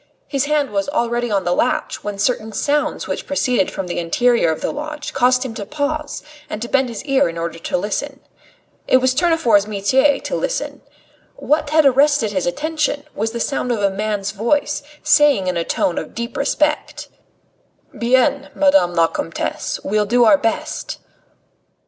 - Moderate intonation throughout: No, wide, 5.9 semitones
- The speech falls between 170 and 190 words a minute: Yes, average, 175 wpm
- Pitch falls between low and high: No, high, 245 Hz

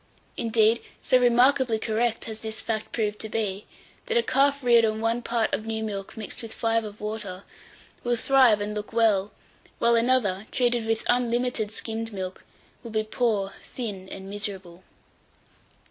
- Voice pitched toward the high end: Yes, high, 225 Hz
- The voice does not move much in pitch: Yes, narrow, 2.1 semitones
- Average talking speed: Yes, average, 160 wpm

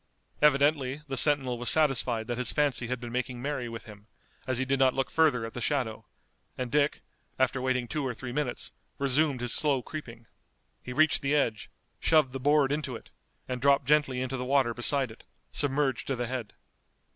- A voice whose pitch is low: Yes, low, 130 Hz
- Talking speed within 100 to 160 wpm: No, average, 195 wpm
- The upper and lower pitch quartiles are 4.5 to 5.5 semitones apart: No, average, 2.8 semitones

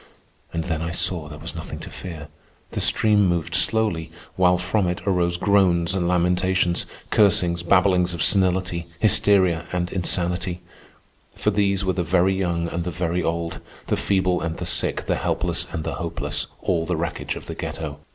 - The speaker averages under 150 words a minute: No, average, 175 wpm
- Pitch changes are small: Yes, narrow, 1.8 semitones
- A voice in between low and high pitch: No, very low, 90 Hz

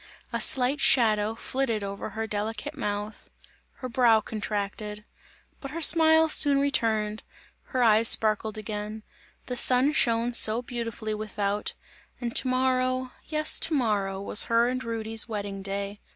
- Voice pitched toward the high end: Yes, high, 225 Hz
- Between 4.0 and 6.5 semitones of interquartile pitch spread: No, average, 3.3 semitones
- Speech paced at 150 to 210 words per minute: No, average, 140 wpm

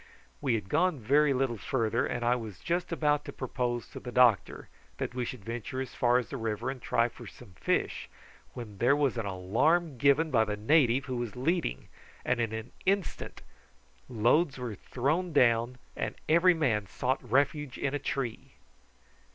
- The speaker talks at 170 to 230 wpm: Yes, average, 180 wpm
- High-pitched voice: No, low, 125 Hz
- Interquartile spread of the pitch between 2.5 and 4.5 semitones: Yes, average, 3.9 semitones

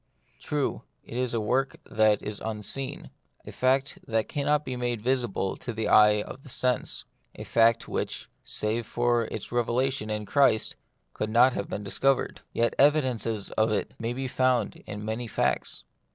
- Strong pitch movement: No, average, 3.1 semitones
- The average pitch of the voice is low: Yes, low, 120 Hz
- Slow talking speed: No, average, 165 wpm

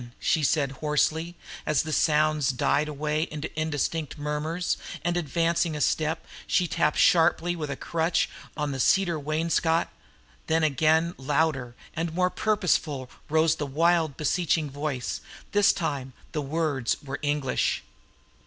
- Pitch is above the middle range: No, medium, 155 Hz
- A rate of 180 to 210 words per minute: No, slow, 135 wpm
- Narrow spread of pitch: Yes, narrow, 2.1 semitones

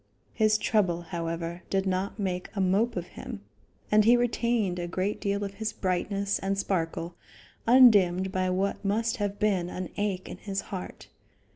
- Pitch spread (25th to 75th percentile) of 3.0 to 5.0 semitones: No, narrow, 2.6 semitones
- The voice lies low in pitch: No, high, 195 Hz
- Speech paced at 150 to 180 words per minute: Yes, average, 165 wpm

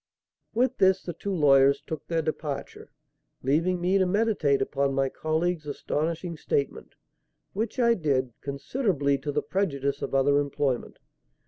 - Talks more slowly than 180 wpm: Yes, average, 140 wpm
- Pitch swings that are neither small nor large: Yes, average, 4.8 semitones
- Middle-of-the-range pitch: Yes, medium, 155 Hz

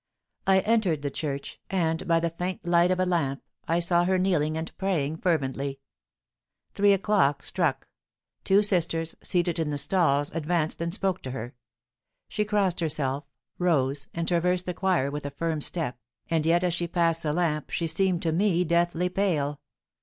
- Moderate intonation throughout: Yes, average, 3.2 semitones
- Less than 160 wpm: No, average, 175 wpm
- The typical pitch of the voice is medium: Yes, medium, 170 Hz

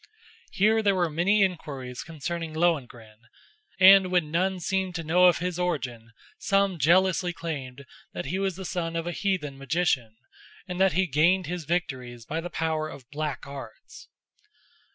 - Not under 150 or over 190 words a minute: Yes, average, 160 wpm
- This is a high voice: No, medium, 170 Hz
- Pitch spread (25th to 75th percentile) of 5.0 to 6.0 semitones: No, average, 4.4 semitones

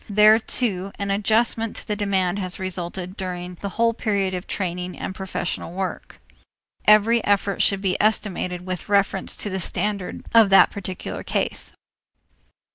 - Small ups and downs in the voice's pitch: Yes, narrow, 2.3 semitones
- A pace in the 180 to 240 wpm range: No, average, 150 wpm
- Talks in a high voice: Yes, high, 195 Hz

